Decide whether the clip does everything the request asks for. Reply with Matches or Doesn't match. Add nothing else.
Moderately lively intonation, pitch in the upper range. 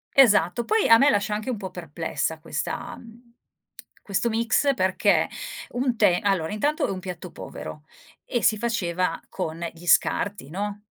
Matches